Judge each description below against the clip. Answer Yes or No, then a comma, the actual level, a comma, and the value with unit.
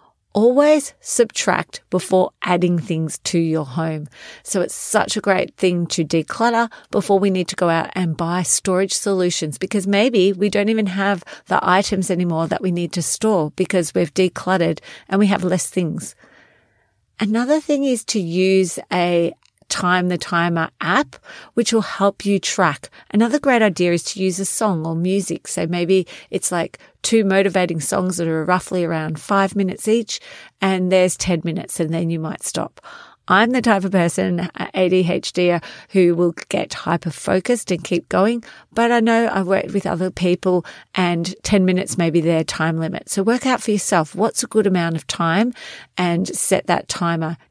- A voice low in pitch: No, medium, 185 Hz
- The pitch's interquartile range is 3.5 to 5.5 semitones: No, average, 3.0 semitones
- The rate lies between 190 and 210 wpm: No, average, 175 wpm